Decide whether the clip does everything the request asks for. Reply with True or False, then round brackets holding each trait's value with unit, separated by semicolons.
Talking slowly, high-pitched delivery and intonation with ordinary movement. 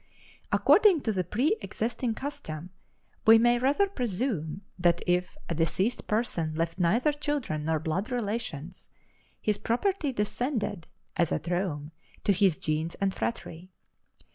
False (130 wpm; 200 Hz; 6.5 semitones)